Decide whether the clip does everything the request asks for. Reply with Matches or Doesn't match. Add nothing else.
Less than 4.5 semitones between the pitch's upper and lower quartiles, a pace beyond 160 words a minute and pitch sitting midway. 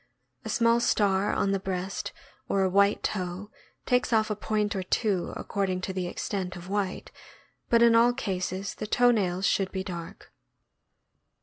Doesn't match